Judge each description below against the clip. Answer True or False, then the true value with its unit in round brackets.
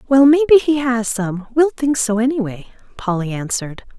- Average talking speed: True (165 wpm)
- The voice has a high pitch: True (245 Hz)